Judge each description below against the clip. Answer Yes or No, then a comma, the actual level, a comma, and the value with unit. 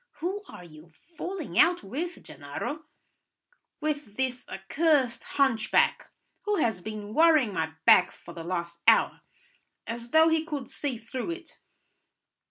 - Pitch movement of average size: No, wide, 8.1 semitones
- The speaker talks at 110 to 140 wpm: Yes, slow, 135 wpm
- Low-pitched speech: No, very high, 260 Hz